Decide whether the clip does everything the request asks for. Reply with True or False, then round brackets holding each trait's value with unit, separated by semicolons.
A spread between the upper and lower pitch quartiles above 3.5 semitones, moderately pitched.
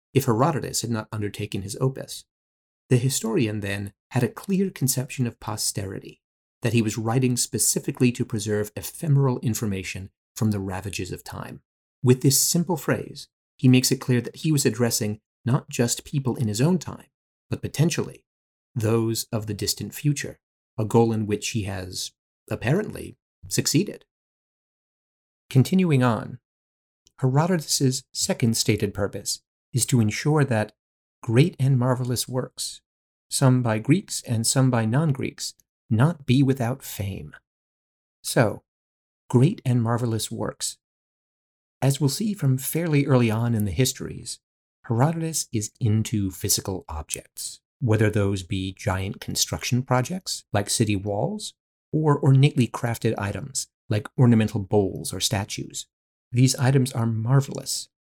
False (4.2 semitones; 120 Hz)